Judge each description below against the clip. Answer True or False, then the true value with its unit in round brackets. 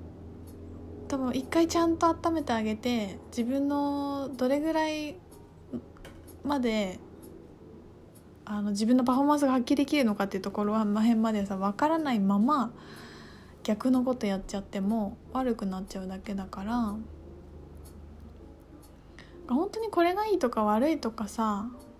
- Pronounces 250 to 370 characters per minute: True (275 characters per minute)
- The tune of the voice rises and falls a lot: True (6.4 semitones)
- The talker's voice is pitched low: False (220 Hz)